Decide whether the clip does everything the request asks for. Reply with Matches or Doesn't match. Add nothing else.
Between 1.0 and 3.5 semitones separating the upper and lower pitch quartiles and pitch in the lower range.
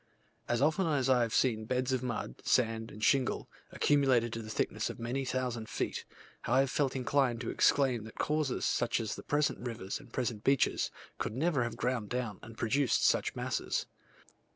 Matches